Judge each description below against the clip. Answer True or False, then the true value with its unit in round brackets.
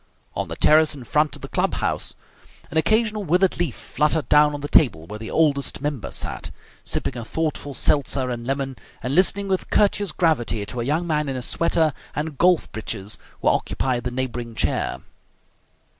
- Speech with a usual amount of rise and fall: True (4.5 semitones)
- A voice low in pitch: False (145 Hz)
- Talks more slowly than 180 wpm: False (185 wpm)